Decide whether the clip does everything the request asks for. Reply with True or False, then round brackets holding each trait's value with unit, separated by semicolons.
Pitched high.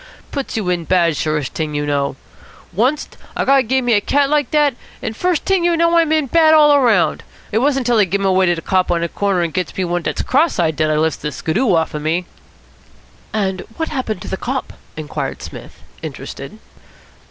True (200 Hz)